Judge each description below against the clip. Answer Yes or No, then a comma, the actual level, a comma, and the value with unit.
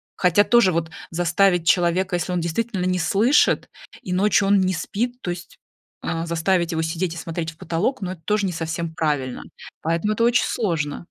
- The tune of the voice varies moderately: Yes, average, 3.2 semitones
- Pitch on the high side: No, medium, 175 Hz